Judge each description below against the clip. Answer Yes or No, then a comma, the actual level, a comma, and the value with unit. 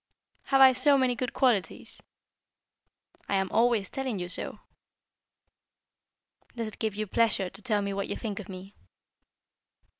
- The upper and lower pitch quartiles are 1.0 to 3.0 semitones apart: No, average, 4.2 semitones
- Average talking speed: Yes, average, 150 wpm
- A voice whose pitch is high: Yes, high, 215 Hz